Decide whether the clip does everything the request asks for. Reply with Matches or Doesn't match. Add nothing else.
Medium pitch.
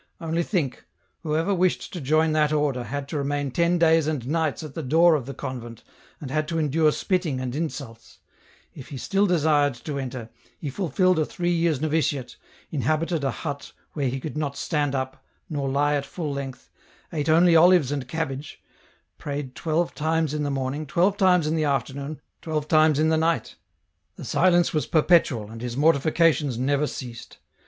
Matches